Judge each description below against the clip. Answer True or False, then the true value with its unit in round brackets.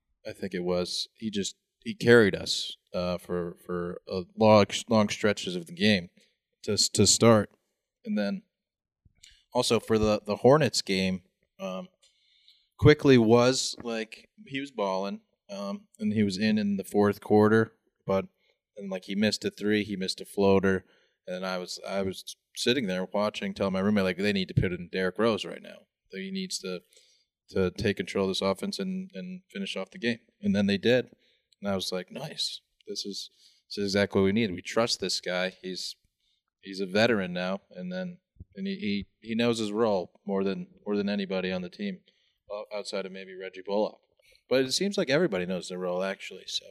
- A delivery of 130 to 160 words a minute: False (195 wpm)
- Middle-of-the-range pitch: False (105 Hz)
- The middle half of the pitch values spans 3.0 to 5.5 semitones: True (4.0 semitones)